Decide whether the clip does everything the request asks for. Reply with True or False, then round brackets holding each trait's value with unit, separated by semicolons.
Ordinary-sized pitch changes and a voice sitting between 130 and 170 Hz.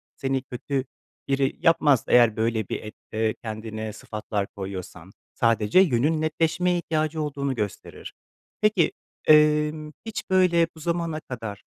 False (6.2 semitones; 135 Hz)